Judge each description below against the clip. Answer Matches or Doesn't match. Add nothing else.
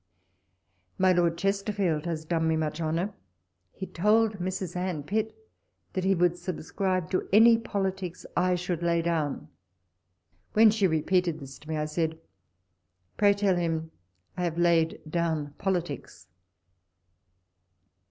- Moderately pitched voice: Matches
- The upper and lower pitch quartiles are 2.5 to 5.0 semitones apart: Matches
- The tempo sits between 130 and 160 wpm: Matches